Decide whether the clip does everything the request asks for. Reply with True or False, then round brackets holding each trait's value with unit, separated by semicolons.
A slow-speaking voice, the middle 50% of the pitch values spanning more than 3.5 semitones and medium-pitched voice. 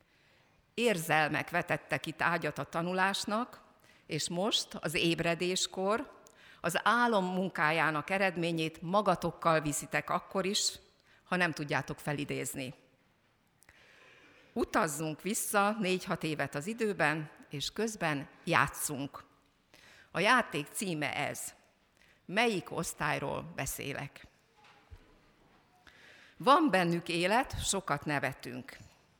True (90 wpm; 4.1 semitones; 170 Hz)